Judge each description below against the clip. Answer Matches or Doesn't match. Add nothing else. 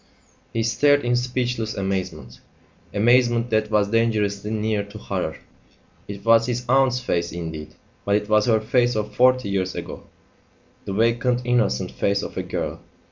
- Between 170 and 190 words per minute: Doesn't match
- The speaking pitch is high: Doesn't match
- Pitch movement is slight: Doesn't match